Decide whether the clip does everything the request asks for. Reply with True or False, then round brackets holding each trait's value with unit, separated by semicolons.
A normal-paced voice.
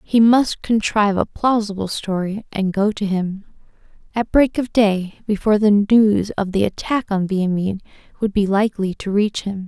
True (175 wpm)